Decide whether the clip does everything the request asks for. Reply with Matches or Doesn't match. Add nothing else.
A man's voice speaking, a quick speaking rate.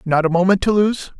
Matches